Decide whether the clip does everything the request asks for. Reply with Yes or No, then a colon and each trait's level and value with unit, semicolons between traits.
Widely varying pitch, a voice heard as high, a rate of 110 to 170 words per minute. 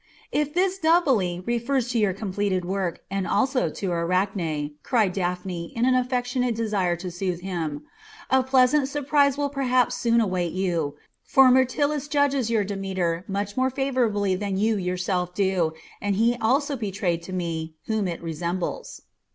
Yes: wide, 6.1 semitones; high, 205 Hz; average, 160 wpm